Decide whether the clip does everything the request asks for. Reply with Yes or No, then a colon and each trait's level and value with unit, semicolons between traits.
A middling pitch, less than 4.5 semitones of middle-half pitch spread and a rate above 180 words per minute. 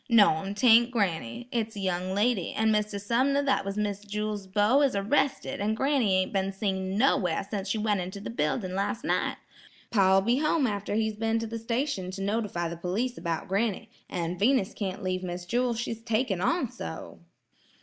No: high, 205 Hz; average, 3.4 semitones; average, 190 wpm